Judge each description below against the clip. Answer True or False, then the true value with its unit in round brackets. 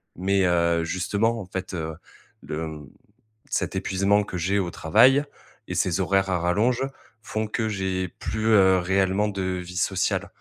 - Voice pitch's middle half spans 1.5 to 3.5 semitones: True (2.8 semitones)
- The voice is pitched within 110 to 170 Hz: False (95 Hz)